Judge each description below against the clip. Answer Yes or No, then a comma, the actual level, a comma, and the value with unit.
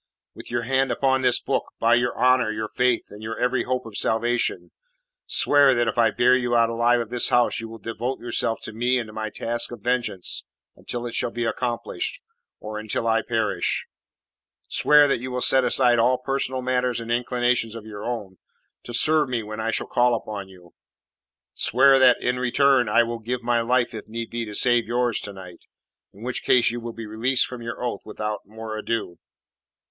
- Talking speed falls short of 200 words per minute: No, fast, 205 wpm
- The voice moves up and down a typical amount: No, narrow, 1.9 semitones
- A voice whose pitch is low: Yes, low, 120 Hz